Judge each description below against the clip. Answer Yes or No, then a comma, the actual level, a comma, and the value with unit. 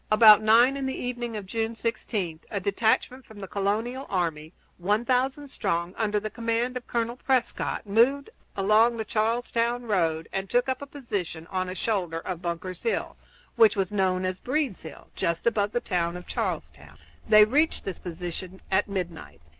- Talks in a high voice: Yes, high, 215 Hz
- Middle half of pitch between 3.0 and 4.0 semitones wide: No, average, 4.5 semitones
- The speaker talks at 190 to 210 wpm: No, average, 175 wpm